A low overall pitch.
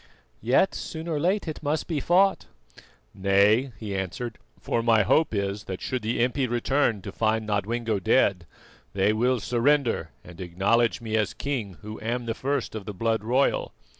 Yes: low, 115 Hz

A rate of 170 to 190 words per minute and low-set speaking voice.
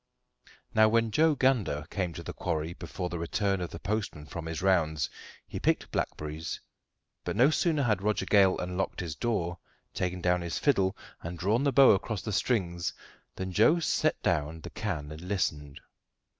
Yes: average, 175 wpm; very low, 95 Hz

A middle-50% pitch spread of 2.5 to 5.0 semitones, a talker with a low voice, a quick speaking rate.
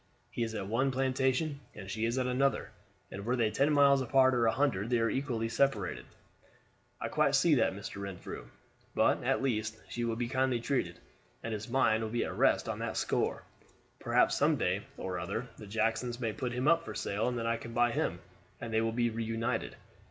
Yes: average, 2.8 semitones; low, 115 Hz; fast, 210 wpm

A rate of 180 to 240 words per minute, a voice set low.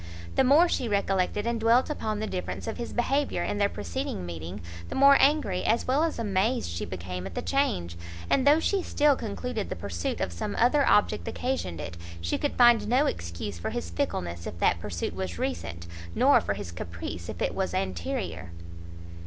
No: average, 195 wpm; high, 195 Hz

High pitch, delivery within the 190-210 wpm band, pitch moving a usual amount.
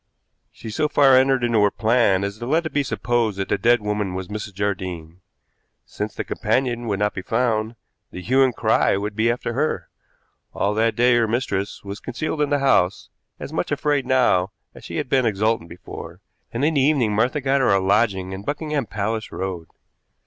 No: low, 110 Hz; average, 200 wpm; average, 4.6 semitones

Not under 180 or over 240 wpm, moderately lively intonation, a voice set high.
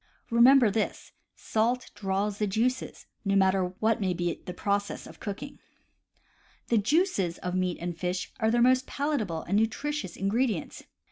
No: average, 155 wpm; average, 4.3 semitones; high, 210 Hz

